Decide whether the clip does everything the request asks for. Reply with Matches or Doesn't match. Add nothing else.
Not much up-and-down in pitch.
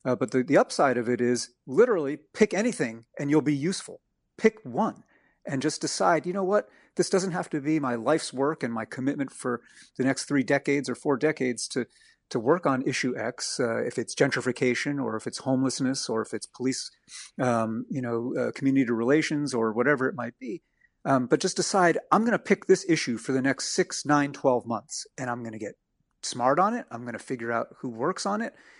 Doesn't match